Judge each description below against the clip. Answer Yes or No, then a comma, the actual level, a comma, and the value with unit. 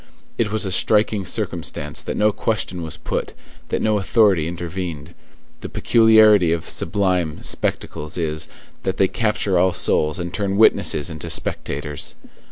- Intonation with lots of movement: No, average, 4.2 semitones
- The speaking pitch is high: No, very low, 95 Hz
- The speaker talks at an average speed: Yes, average, 145 wpm